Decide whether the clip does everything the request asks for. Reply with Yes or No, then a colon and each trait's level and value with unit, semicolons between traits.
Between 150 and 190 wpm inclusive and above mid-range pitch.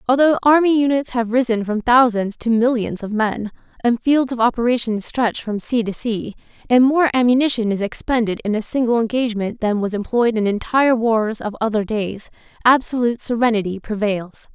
Yes: average, 170 wpm; high, 230 Hz